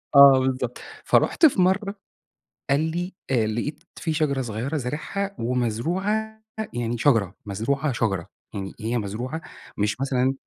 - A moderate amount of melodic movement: No, wide, 5.8 semitones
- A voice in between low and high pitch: No, low, 130 Hz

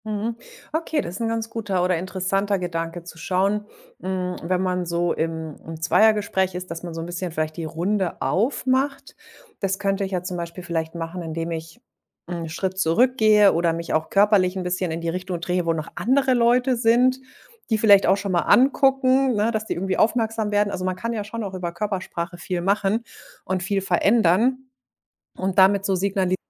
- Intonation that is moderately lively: Yes, average, 3.9 semitones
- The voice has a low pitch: No, high, 190 Hz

